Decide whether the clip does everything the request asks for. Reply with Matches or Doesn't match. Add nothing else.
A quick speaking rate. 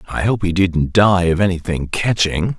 Doesn't match